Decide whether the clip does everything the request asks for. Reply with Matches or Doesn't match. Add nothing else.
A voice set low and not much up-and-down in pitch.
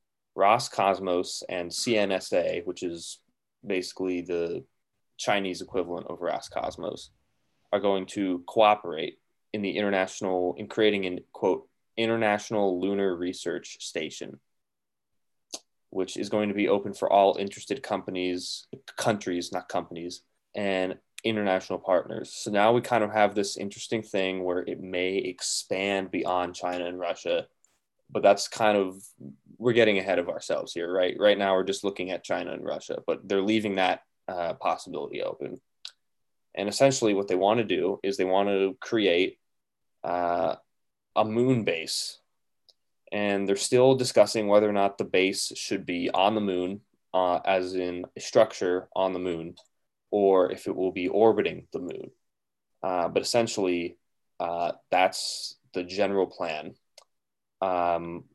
Matches